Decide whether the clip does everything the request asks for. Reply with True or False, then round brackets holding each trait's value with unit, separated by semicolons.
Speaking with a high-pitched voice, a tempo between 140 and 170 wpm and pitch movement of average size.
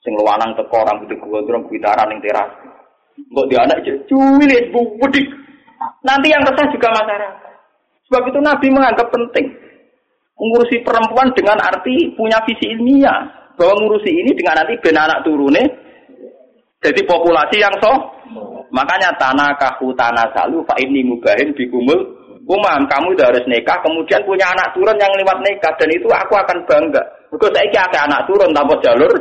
False (235 Hz; 155 wpm; 7.1 semitones)